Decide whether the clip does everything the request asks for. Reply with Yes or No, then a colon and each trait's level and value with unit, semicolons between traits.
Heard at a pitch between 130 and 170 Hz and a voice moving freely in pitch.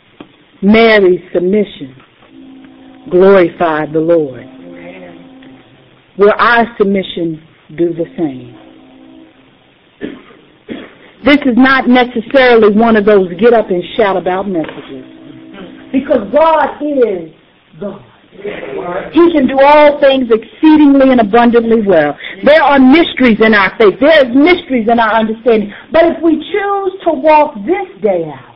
No: high, 225 Hz; wide, 8.2 semitones